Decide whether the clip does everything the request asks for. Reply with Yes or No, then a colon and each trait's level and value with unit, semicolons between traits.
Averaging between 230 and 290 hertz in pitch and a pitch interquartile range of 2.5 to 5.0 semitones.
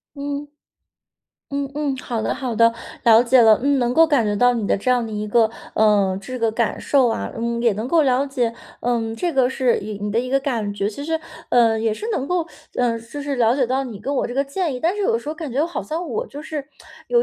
Yes: very high, 250 Hz; average, 4.0 semitones